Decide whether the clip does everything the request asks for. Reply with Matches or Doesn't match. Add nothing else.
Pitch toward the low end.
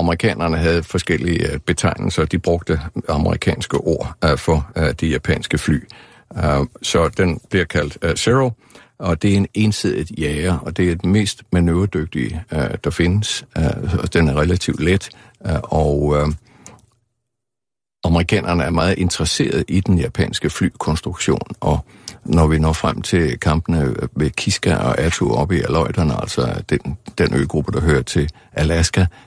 Matches